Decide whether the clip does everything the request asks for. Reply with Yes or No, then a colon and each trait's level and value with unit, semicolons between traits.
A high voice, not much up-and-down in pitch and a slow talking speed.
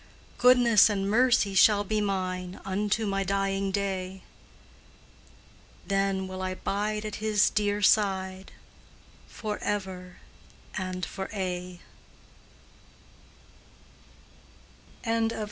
Yes: high, 195 Hz; narrow, 1.9 semitones; slow, 85 wpm